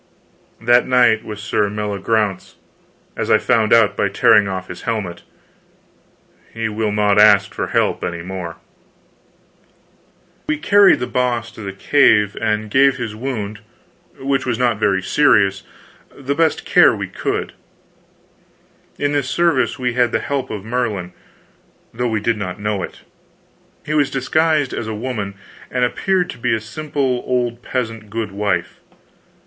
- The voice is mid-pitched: No, low, 115 Hz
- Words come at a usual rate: Yes, average, 150 wpm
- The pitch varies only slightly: No, average, 3.7 semitones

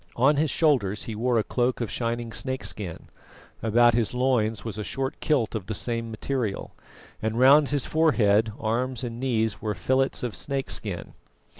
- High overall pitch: No, low, 120 Hz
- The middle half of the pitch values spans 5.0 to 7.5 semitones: No, average, 3.2 semitones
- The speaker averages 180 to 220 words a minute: No, average, 165 wpm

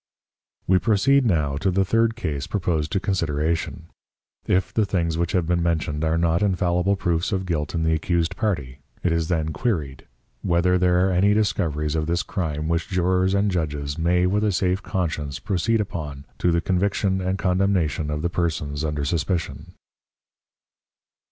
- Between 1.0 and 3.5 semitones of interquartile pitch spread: Yes, average, 3.2 semitones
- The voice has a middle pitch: No, very low, 85 Hz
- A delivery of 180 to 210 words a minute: No, average, 170 wpm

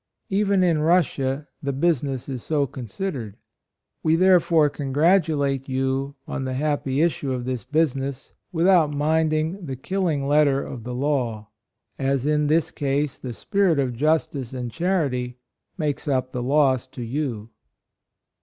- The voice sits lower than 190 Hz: Yes, medium, 140 Hz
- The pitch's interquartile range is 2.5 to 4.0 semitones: Yes, average, 3.4 semitones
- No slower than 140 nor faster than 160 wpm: Yes, average, 145 wpm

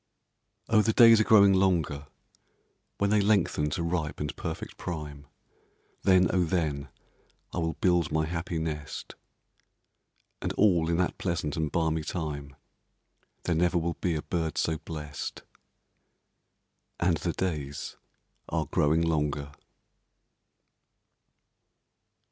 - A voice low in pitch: Yes, very low, 80 Hz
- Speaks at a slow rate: Yes, slow, 120 wpm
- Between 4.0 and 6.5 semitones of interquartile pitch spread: No, average, 3.1 semitones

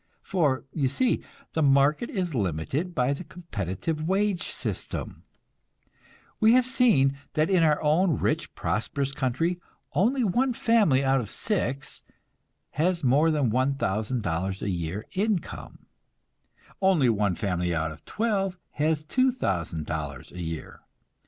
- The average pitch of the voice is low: No, medium, 145 Hz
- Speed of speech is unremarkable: No, slow, 125 wpm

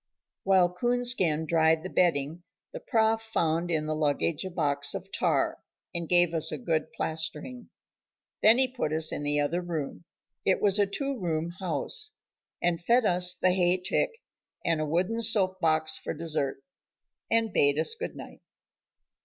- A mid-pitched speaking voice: Yes, medium, 175 Hz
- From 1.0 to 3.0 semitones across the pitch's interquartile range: No, average, 4.4 semitones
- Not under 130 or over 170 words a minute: Yes, average, 165 wpm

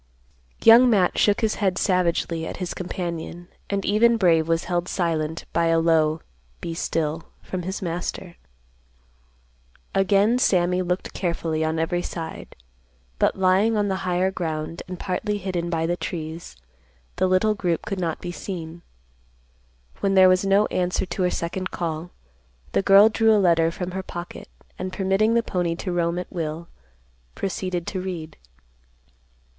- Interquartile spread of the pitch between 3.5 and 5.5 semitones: No, narrow, 2.4 semitones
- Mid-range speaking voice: Yes, medium, 180 Hz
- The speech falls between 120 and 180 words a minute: Yes, average, 155 wpm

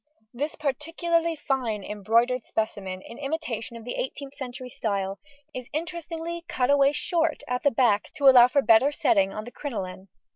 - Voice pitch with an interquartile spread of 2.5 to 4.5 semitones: No, average, 5.1 semitones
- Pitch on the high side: Yes, very high, 255 Hz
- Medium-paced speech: Yes, average, 160 wpm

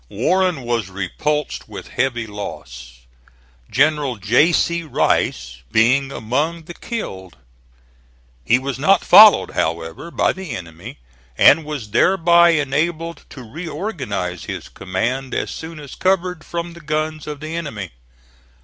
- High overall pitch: No, medium, 140 Hz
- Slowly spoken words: Yes, slow, 130 wpm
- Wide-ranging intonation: Yes, wide, 7.9 semitones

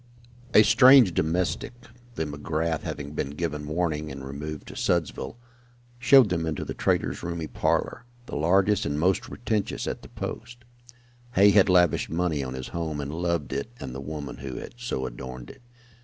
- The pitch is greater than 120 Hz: No, very low, 80 Hz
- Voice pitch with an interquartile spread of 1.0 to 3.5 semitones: No, average, 4.7 semitones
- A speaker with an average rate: Yes, average, 170 wpm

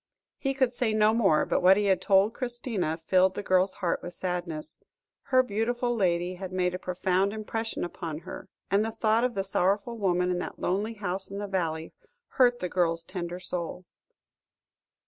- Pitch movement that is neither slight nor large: Yes, average, 3.6 semitones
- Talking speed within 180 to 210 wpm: Yes, average, 185 wpm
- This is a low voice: No, high, 190 Hz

